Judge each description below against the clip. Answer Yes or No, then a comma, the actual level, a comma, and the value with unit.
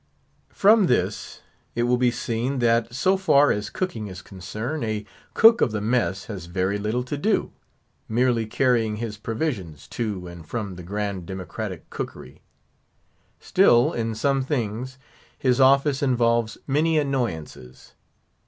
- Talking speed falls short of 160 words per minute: Yes, average, 140 wpm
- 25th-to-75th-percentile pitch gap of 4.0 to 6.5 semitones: Yes, average, 4.3 semitones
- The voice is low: Yes, low, 115 Hz